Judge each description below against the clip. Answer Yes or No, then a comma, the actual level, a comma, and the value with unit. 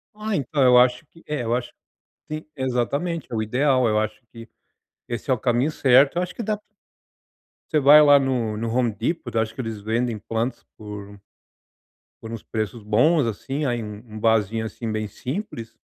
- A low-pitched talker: Yes, low, 120 Hz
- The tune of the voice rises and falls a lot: No, average, 4.1 semitones